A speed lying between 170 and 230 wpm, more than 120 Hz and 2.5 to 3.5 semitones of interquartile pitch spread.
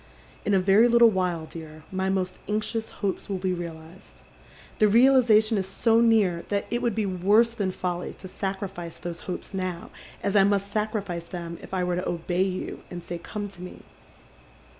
Yes: average, 185 wpm; high, 190 Hz; average, 3.1 semitones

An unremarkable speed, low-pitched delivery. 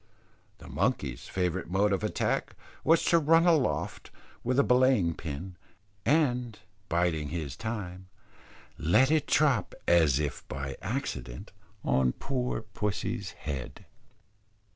No: slow, 120 wpm; very low, 95 Hz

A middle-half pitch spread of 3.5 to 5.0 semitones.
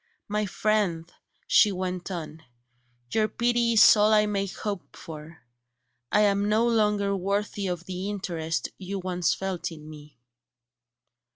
No: average, 3.1 semitones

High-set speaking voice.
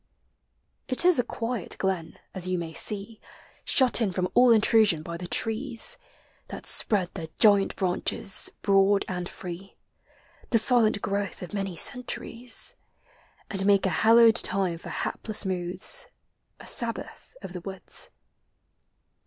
Yes: high, 200 Hz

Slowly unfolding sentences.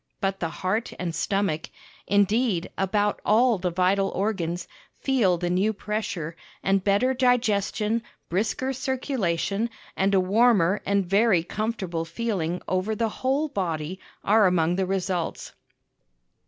Yes: slow, 130 wpm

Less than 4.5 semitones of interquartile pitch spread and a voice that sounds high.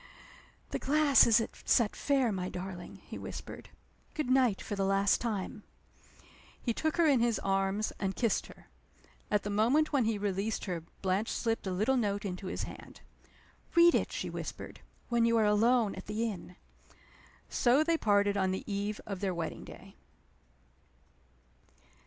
Yes: average, 3.6 semitones; high, 210 Hz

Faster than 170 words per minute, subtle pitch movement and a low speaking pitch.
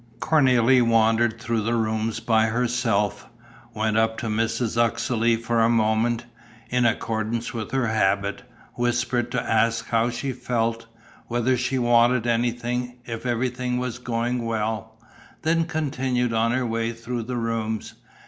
No: average, 140 wpm; narrow, 1.5 semitones; low, 115 Hz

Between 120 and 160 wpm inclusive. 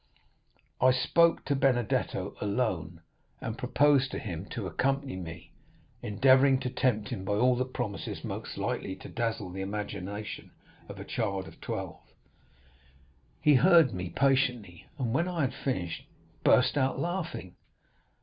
Yes: average, 140 wpm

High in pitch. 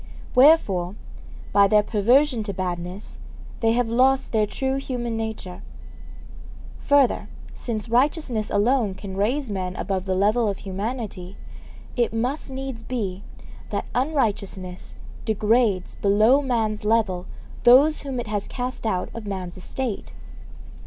Yes: high, 220 Hz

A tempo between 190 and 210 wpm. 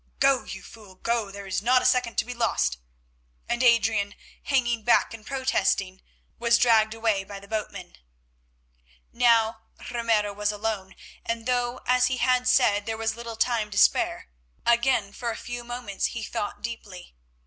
No: average, 165 wpm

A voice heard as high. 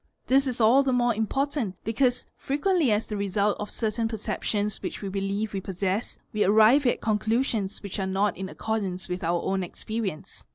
Yes: high, 215 Hz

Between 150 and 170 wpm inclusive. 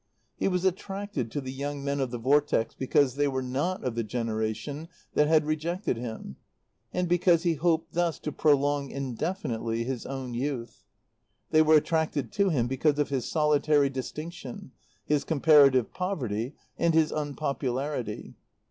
Yes: average, 155 wpm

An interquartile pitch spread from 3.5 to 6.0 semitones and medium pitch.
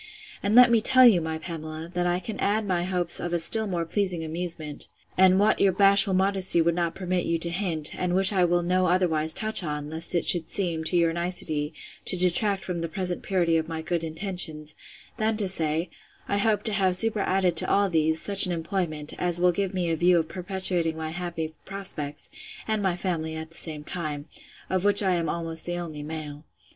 No: average, 2.8 semitones; medium, 175 Hz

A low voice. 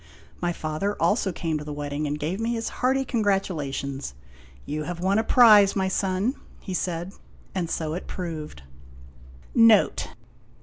No: medium, 180 Hz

